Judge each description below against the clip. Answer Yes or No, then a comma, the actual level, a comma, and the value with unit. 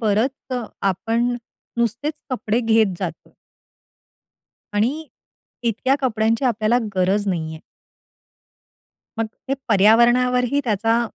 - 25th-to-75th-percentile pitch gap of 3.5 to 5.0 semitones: No, average, 2.7 semitones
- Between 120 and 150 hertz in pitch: No, high, 230 Hz